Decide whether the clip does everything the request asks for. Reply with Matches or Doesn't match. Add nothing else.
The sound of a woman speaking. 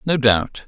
Doesn't match